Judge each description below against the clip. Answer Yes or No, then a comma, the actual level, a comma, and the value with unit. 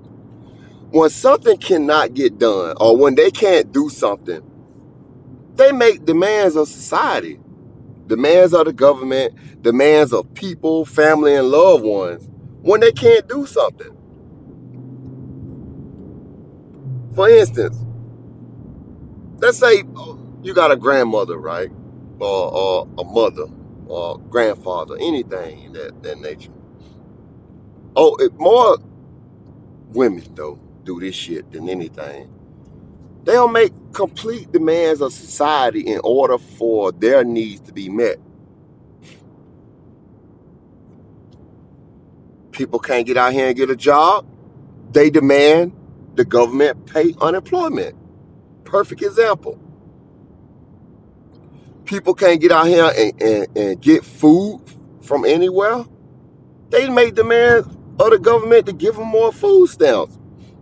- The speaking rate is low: Yes, slow, 115 wpm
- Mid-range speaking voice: No, high, 200 Hz